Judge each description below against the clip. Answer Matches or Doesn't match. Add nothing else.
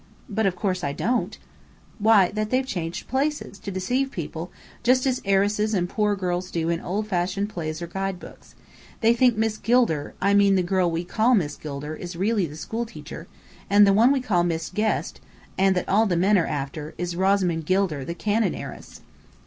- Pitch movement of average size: Matches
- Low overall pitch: Doesn't match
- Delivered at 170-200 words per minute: Matches